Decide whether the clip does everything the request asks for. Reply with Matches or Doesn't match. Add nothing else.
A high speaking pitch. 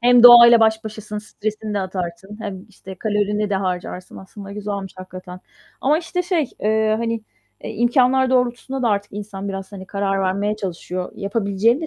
Matches